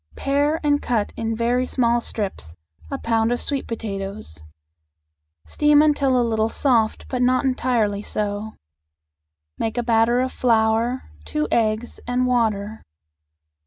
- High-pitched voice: Yes, high, 230 Hz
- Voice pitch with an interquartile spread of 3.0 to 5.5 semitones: No, narrow, 2.6 semitones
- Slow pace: Yes, slow, 130 wpm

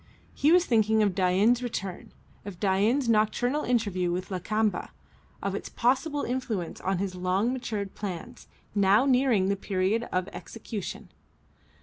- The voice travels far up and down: No, average, 4.3 semitones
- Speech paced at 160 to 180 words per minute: No, average, 140 wpm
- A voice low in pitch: No, high, 210 Hz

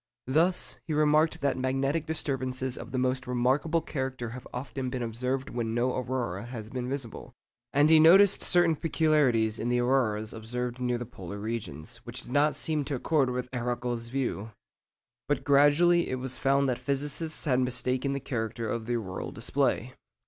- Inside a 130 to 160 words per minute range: No, average, 170 wpm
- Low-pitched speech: Yes, low, 130 Hz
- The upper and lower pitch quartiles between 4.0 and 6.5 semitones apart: No, average, 3.0 semitones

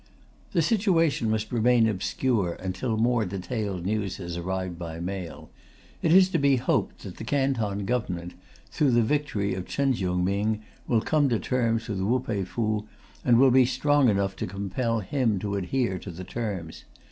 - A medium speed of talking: Yes, average, 175 wpm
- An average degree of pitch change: Yes, average, 5.0 semitones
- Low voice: Yes, low, 110 Hz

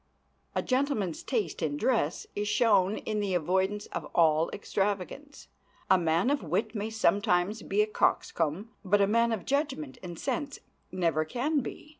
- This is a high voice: Yes, high, 205 Hz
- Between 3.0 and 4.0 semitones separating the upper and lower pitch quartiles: No, average, 4.8 semitones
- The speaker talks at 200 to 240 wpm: No, average, 160 wpm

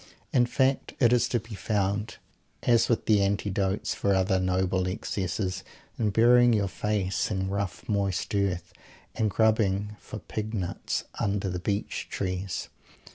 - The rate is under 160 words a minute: Yes, average, 145 wpm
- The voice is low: Yes, low, 100 Hz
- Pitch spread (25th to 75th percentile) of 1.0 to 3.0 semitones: Yes, narrow, 2.6 semitones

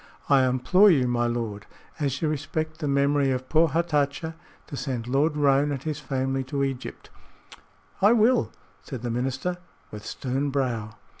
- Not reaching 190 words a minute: Yes, average, 160 wpm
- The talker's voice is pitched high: No, medium, 140 Hz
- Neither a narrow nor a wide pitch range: Yes, average, 3.1 semitones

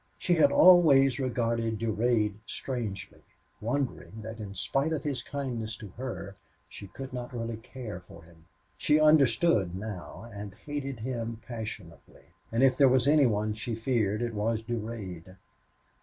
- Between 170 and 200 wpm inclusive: No, average, 150 wpm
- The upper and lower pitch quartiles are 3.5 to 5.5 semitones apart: Yes, average, 3.9 semitones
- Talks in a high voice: No, low, 115 Hz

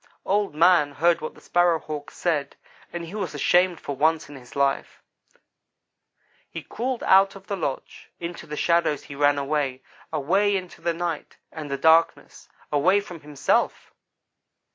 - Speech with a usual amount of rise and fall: Yes, average, 3.6 semitones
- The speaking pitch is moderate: Yes, medium, 165 Hz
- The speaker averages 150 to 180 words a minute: Yes, average, 160 wpm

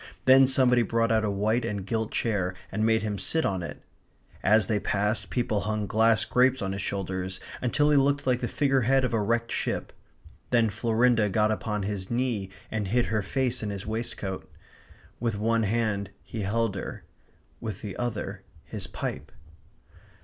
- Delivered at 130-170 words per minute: No, average, 180 wpm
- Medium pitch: No, low, 110 Hz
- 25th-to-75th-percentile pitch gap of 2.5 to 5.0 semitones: Yes, average, 3.0 semitones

